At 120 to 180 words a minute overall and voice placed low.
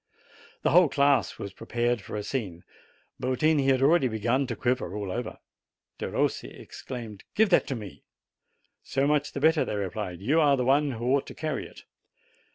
No: average, 195 wpm; low, 130 Hz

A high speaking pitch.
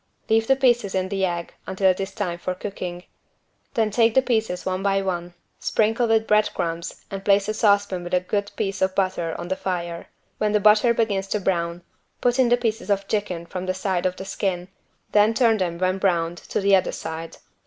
Yes: high, 195 Hz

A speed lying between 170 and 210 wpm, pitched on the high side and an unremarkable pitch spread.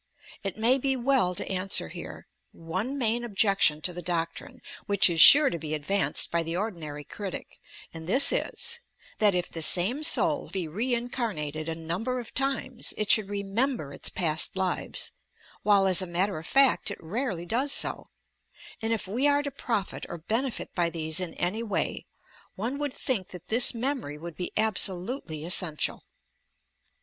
No: average, 175 wpm; high, 195 Hz; wide, 6.2 semitones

